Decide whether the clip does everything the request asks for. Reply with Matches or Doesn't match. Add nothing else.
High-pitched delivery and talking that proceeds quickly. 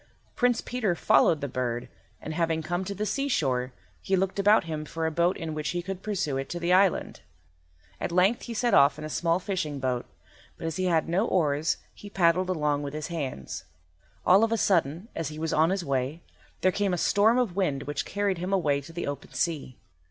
Doesn't match